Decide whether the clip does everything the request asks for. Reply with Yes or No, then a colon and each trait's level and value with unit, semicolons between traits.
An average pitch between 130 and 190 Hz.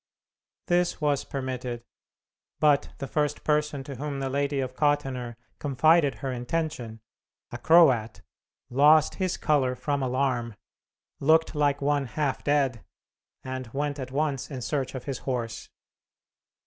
Yes: medium, 140 Hz